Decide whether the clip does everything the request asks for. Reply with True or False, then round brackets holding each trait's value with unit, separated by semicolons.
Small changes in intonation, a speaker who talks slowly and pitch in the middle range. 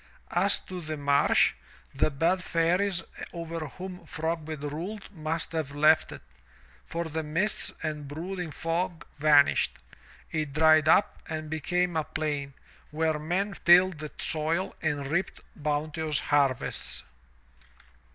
True (2.3 semitones; 125 wpm; 160 Hz)